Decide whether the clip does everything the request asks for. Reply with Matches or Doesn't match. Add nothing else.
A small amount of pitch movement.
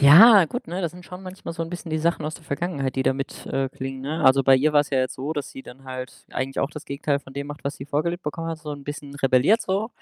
Doesn't match